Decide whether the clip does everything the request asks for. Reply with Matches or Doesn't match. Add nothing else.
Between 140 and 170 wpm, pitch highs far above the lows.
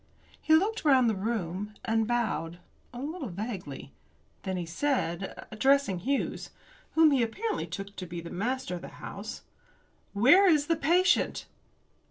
Matches